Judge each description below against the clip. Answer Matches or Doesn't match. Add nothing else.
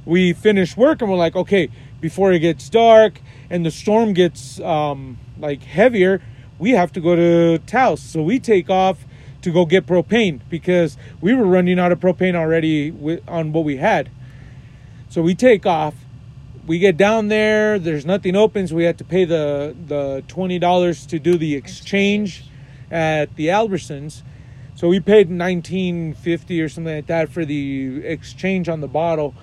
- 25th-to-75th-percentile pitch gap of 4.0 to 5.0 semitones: Matches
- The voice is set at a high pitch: Doesn't match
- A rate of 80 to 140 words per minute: Doesn't match